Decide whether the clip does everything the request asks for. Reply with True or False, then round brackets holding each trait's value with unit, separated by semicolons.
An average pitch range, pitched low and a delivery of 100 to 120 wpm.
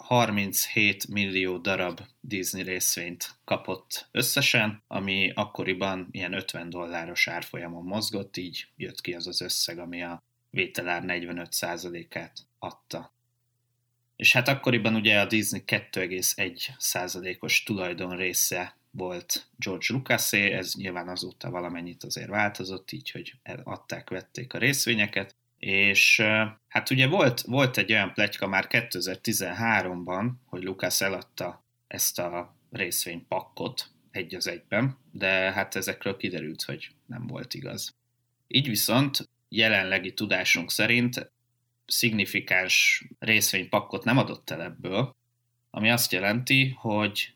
True (4.7 semitones; 105 Hz; 115 wpm)